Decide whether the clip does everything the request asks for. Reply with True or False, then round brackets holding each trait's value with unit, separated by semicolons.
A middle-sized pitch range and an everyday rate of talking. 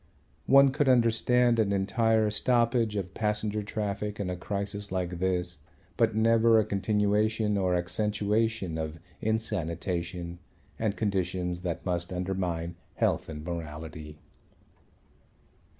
False (3.8 semitones; 115 wpm)